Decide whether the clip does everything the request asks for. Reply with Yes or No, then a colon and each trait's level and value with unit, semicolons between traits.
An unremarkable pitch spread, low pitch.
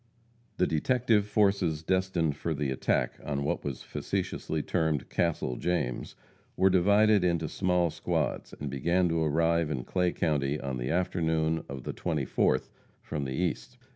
Yes: average, 3.7 semitones; very low, 80 Hz